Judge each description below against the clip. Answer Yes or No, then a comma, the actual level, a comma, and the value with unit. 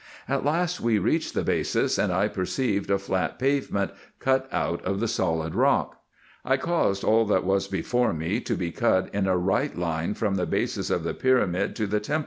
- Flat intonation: No, average, 5.2 semitones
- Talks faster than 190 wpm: Yes, average, 200 wpm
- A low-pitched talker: Yes, low, 100 Hz